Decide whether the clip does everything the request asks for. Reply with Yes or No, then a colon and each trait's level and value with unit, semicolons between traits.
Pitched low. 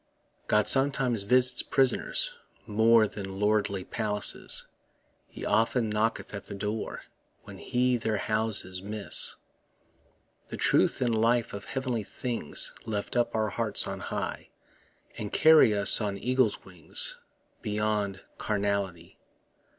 Yes: low, 110 Hz